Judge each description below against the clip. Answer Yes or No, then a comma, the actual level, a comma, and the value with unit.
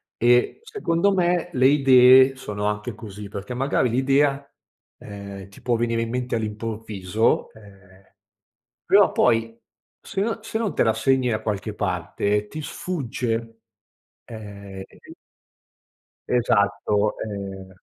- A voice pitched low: Yes, low, 115 Hz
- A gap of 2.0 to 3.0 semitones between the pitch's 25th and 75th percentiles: No, average, 4.4 semitones